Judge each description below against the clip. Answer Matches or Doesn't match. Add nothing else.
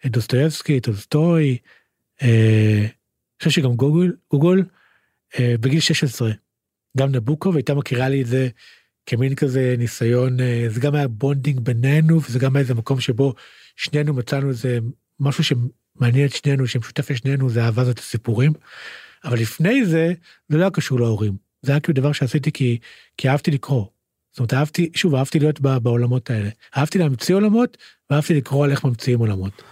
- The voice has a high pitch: Doesn't match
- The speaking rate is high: Matches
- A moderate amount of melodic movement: Matches